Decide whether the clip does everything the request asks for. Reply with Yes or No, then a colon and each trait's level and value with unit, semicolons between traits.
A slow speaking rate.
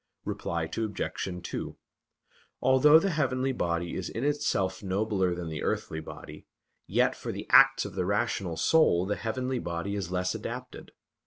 No: average, 155 wpm